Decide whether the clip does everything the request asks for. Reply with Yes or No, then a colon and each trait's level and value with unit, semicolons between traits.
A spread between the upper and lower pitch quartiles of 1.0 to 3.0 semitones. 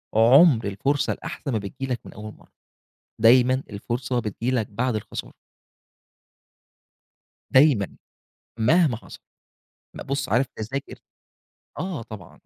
No: average, 3.7 semitones